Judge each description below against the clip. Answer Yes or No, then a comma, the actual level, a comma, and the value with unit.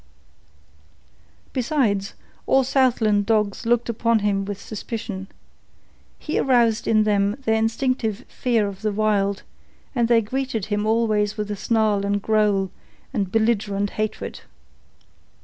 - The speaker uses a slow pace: Yes, slow, 120 wpm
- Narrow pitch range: Yes, narrow, 2.3 semitones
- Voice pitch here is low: No, high, 215 Hz